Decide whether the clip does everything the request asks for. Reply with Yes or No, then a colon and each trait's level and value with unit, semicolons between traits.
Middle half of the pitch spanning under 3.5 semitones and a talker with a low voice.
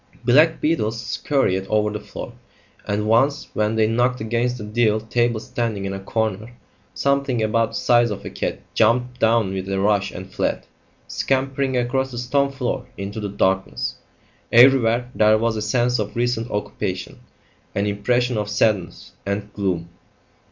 Yes: average, 2.9 semitones; low, 115 Hz